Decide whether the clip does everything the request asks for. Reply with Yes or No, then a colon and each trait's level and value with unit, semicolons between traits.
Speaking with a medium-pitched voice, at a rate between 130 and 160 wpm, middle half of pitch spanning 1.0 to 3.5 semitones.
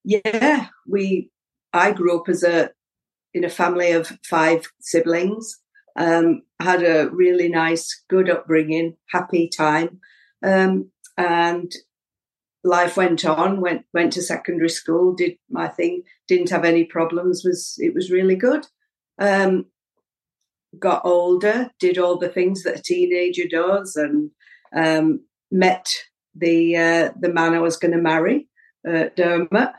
Yes: medium, 175 Hz; average, 140 wpm; average, 2.7 semitones